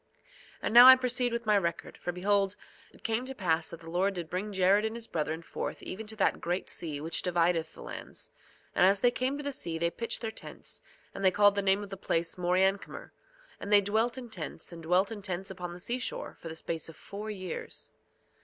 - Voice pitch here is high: Yes, high, 195 Hz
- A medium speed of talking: No, fast, 230 wpm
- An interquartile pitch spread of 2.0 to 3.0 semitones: No, average, 4.2 semitones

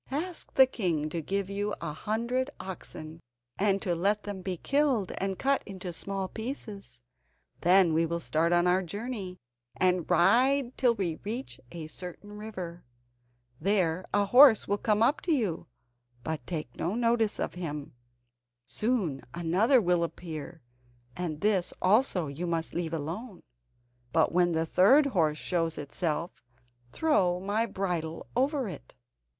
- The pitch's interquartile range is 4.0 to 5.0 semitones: Yes, average, 4.7 semitones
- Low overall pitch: No, medium, 185 Hz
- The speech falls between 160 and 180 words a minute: No, average, 145 wpm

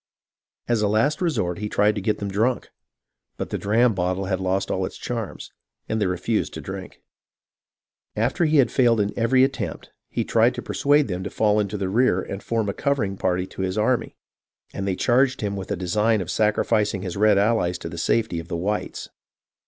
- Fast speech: Yes, fast, 210 wpm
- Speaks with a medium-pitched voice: No, low, 105 Hz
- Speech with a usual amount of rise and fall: Yes, average, 3.5 semitones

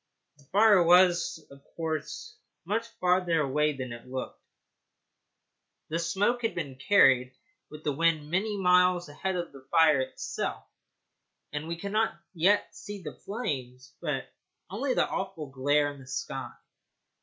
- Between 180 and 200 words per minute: No, average, 145 wpm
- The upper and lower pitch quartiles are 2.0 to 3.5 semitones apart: No, average, 5.0 semitones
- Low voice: No, medium, 165 Hz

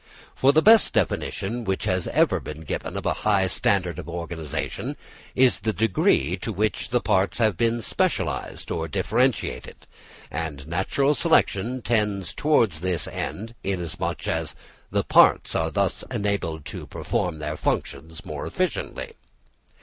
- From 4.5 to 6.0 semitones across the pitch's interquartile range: Yes, wide, 5.4 semitones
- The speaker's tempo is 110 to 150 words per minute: Yes, average, 140 wpm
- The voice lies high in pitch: No, low, 100 Hz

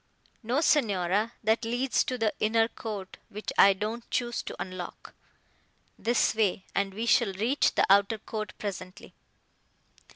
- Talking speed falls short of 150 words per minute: Yes, average, 140 wpm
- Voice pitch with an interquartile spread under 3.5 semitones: Yes, average, 3.0 semitones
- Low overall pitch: No, high, 220 Hz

